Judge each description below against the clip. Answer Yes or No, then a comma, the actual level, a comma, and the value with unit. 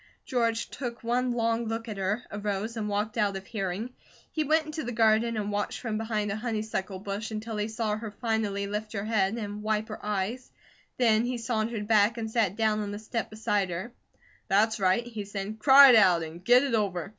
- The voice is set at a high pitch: Yes, high, 215 Hz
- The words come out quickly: Yes, fast, 210 wpm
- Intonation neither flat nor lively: No, narrow, 2.1 semitones